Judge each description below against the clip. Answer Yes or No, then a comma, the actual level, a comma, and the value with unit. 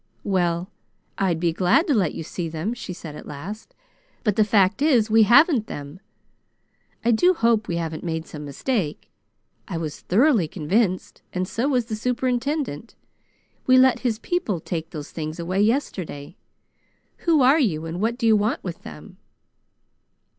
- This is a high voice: Yes, high, 205 Hz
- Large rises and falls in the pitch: Yes, wide, 6.4 semitones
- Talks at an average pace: Yes, average, 165 wpm